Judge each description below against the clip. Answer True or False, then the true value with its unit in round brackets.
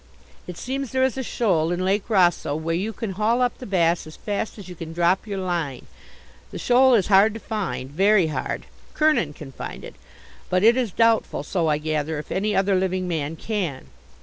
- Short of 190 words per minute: False (205 wpm)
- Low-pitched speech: False (190 Hz)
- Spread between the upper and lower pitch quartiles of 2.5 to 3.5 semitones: False (5.0 semitones)